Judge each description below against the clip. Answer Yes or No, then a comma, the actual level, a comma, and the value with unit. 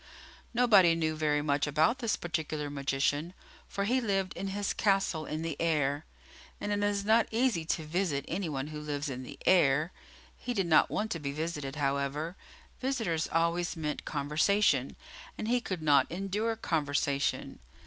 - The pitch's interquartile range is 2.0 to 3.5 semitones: No, average, 5.2 semitones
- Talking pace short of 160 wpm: No, average, 165 wpm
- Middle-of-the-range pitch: Yes, medium, 165 Hz